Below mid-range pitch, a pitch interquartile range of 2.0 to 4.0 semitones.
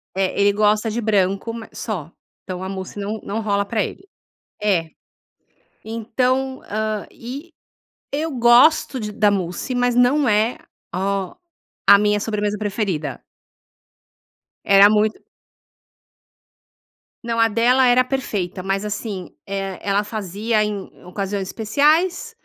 No: high, 210 Hz; average, 3.1 semitones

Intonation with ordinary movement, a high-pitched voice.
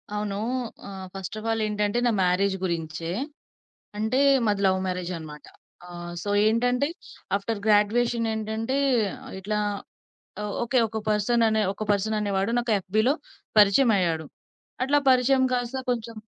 Yes: average, 3.3 semitones; high, 210 Hz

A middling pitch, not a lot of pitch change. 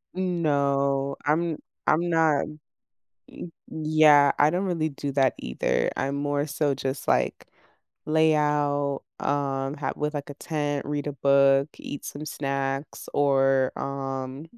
Yes: medium, 145 Hz; narrow, 1.8 semitones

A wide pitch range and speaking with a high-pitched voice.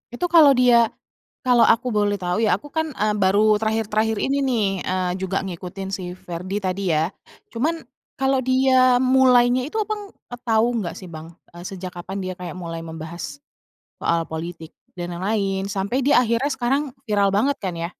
Yes: wide, 5.8 semitones; high, 205 Hz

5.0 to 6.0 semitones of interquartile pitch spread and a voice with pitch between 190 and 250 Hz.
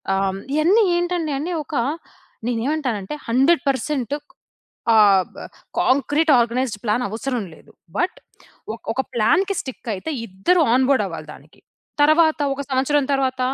No: average, 5.3 semitones; very high, 265 Hz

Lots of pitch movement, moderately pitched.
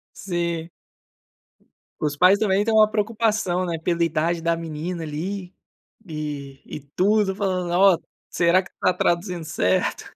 No: average, 2.8 semitones; medium, 175 Hz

